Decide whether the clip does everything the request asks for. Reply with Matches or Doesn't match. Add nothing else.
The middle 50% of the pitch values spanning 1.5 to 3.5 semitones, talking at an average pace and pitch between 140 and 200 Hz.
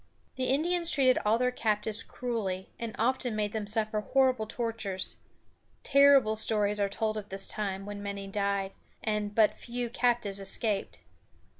Doesn't match